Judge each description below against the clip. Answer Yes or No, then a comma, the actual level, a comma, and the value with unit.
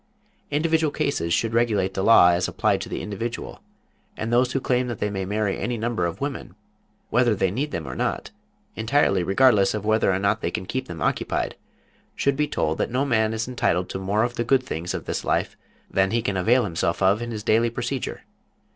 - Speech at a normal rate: No, fast, 215 wpm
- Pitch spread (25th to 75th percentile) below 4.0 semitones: No, average, 4.3 semitones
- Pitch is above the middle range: No, low, 110 Hz